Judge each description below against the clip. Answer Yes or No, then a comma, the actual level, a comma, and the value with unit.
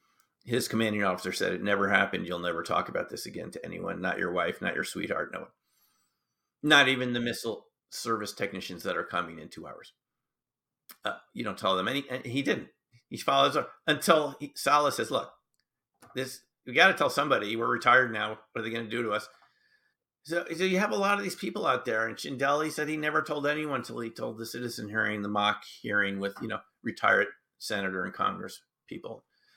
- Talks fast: Yes, fast, 215 wpm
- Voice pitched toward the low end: Yes, low, 120 Hz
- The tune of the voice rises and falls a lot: Yes, wide, 5.9 semitones